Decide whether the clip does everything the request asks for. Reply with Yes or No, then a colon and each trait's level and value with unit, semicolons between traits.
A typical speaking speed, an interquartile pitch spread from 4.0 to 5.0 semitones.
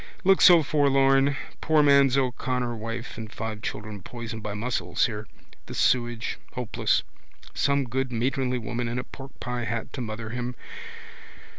No: average, 145 wpm; average, 3.0 semitones